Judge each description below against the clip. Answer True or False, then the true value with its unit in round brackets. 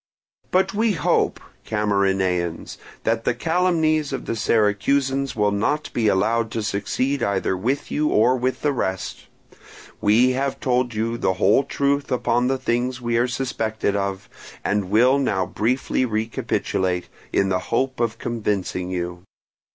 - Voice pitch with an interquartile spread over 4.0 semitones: True (4.6 semitones)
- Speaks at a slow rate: False (145 wpm)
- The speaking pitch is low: True (115 Hz)